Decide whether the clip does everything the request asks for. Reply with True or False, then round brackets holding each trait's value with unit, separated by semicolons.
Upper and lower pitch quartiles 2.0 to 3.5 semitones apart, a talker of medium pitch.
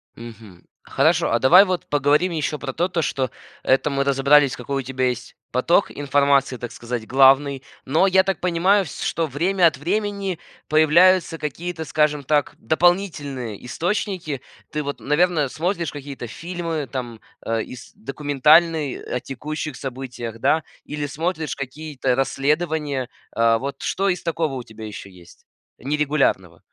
False (4.2 semitones; 145 Hz)